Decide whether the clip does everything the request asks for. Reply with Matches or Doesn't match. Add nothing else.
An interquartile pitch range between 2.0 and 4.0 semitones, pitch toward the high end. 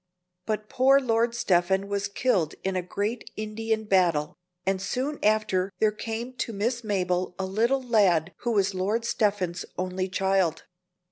Matches